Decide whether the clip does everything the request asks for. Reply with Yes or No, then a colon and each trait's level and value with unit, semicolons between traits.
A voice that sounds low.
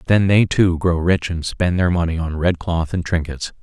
Yes: very low, 85 Hz